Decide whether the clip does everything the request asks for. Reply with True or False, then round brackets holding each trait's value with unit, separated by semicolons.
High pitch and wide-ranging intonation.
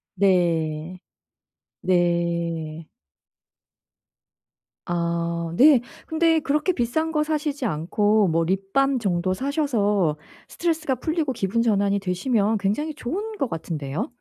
True (200 Hz; 8.6 semitones)